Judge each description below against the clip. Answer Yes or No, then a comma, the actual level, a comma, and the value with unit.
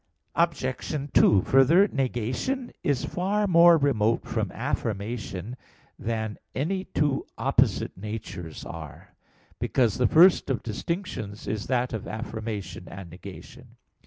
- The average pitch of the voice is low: Yes, low, 125 Hz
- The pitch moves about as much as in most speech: No, wide, 6.9 semitones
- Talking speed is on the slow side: Yes, slow, 115 wpm